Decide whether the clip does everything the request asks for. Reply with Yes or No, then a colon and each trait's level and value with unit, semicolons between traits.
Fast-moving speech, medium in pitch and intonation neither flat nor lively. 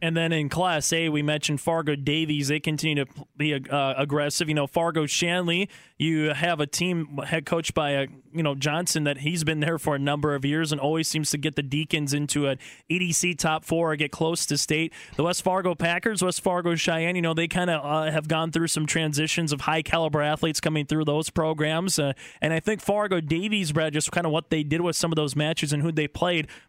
No: fast, 235 wpm; medium, 155 Hz; narrow, 2.1 semitones